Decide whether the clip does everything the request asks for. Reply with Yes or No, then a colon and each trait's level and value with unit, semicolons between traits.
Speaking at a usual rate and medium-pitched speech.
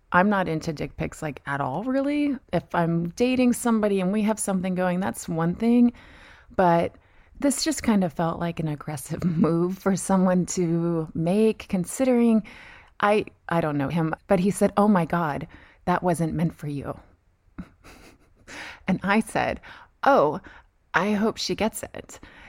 Yes: average, 165 wpm; medium, 180 Hz